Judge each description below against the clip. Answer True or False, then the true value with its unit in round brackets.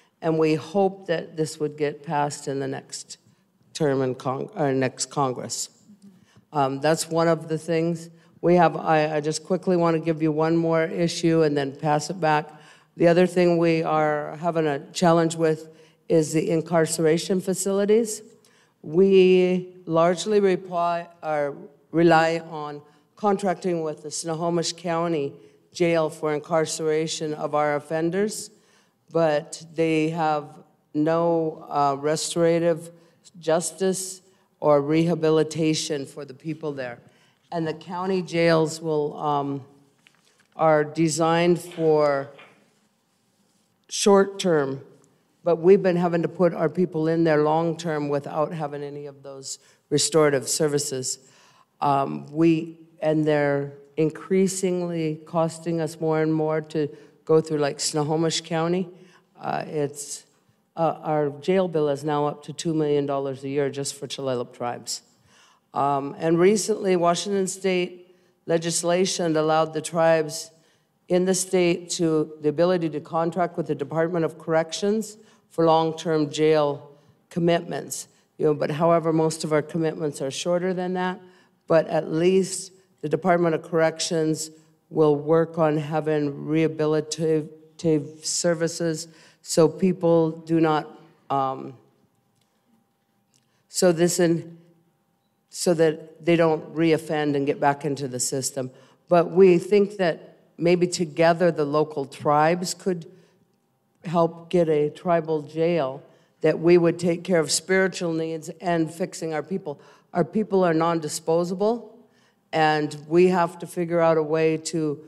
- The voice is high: False (160 Hz)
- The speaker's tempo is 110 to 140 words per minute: True (135 wpm)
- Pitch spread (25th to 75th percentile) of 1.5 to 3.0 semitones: True (2.4 semitones)